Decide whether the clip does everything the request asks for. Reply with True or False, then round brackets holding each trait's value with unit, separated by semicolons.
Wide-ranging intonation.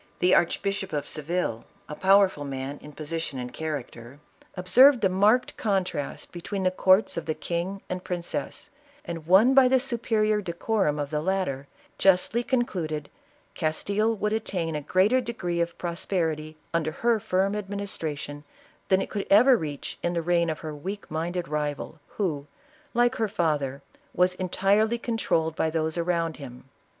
False (4.5 semitones)